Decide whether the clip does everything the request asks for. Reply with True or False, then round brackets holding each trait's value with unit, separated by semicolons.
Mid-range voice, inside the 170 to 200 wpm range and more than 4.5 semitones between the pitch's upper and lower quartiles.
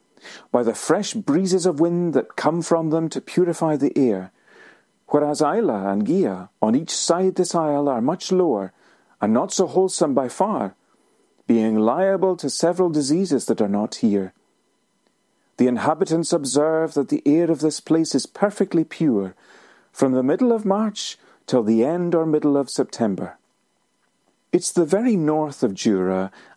False (160 Hz; 160 wpm; 5.1 semitones)